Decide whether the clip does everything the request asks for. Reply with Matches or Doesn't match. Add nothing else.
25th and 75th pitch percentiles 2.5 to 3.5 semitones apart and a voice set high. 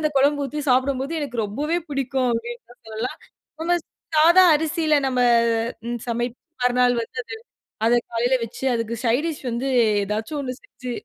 Doesn't match